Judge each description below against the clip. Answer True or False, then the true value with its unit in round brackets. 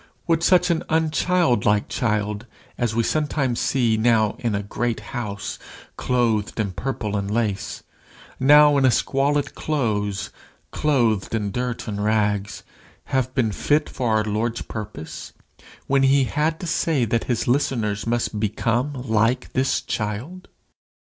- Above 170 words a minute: False (140 wpm)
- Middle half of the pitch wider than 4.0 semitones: True (4.4 semitones)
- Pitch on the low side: True (120 Hz)